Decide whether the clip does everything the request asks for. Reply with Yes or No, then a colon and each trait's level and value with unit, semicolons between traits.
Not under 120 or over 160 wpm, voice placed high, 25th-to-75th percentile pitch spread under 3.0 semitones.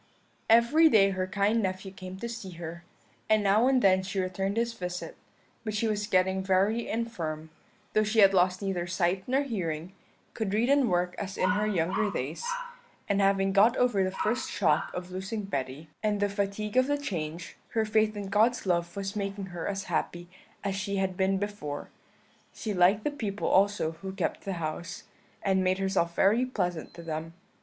No: average, 190 wpm; high, 195 Hz; narrow, 2.6 semitones